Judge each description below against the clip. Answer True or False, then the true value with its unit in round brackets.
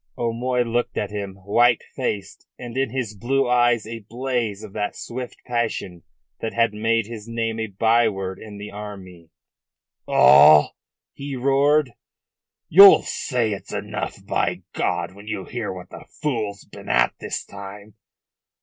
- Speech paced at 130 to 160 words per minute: True (150 wpm)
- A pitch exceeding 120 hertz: False (115 Hz)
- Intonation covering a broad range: False (3.2 semitones)